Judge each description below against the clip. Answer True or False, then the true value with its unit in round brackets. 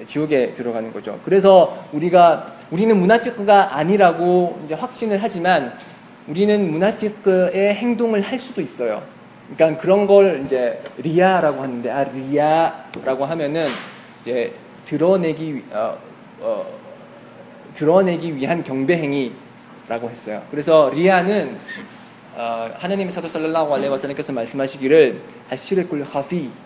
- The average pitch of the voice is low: False (170 Hz)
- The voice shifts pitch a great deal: True (5.8 semitones)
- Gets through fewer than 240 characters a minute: False (295 characters per minute)